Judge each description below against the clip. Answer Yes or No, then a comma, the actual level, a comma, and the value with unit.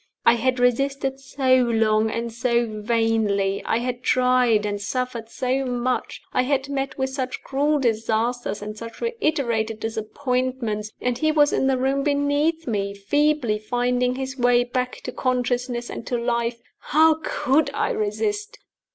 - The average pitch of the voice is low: No, very high, 250 Hz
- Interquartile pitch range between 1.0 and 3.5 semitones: Yes, average, 2.9 semitones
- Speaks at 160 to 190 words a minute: No, average, 150 wpm